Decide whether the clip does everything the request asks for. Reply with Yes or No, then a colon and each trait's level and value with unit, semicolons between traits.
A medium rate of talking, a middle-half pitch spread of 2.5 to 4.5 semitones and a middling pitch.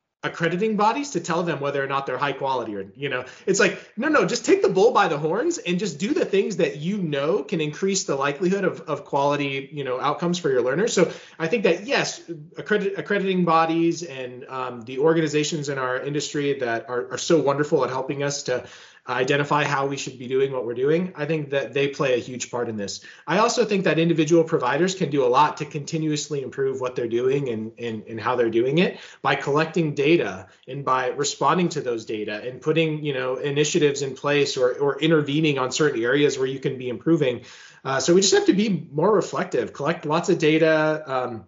No: fast, 220 wpm; average, 4.1 semitones; medium, 150 Hz